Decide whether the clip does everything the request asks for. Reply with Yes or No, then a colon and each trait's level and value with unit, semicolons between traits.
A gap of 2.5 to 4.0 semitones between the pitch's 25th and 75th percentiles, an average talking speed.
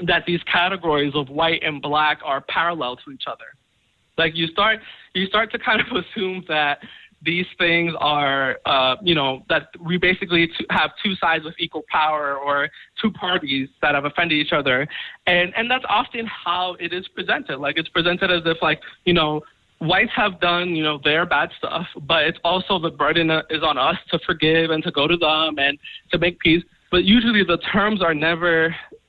Yes: average, 2.9 semitones; average, 195 wpm